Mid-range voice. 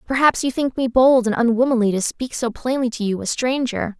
No: high, 245 Hz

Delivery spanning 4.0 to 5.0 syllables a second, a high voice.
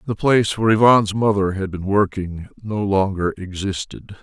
No: 4.9 syllables/s; low, 100 Hz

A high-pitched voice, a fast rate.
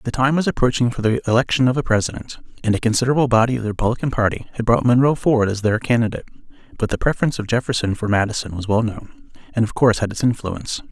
No: low, 115 Hz; fast, 225 wpm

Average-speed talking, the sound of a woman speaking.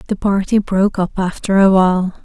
Yes: average, 190 wpm; female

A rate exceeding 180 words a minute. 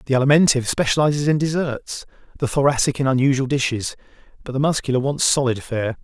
No: average, 160 wpm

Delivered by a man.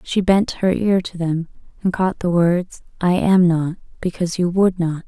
No: female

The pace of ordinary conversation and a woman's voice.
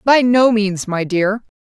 Yes: average, 185 wpm; female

